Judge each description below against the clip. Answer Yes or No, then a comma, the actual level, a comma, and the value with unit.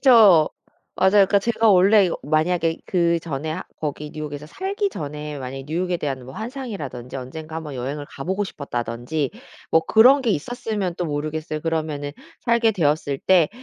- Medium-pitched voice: Yes, medium, 160 Hz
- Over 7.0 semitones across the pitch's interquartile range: No, average, 5.2 semitones